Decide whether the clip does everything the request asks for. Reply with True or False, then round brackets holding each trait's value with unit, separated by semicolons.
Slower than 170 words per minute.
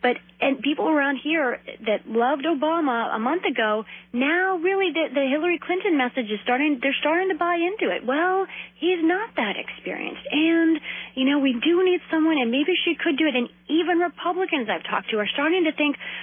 False (200 wpm)